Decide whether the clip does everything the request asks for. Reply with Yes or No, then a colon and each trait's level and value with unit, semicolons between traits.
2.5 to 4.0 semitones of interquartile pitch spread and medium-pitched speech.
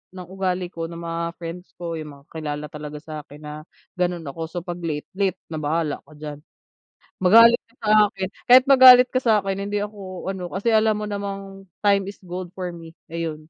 Yes: average, 3.6 semitones; medium, 180 Hz